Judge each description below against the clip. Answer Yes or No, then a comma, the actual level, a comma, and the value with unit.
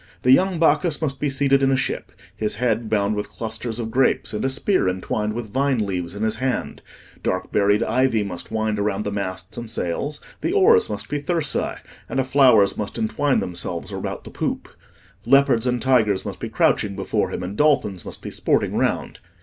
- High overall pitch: No, low, 115 Hz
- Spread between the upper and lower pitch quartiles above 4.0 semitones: Yes, average, 5.1 semitones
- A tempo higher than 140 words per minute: Yes, average, 195 wpm